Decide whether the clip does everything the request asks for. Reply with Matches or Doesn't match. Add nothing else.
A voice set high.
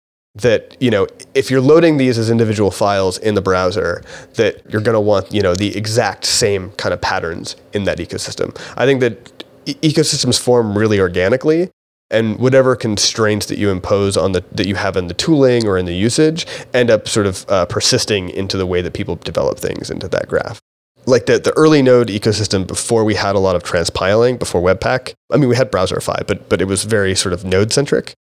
Doesn't match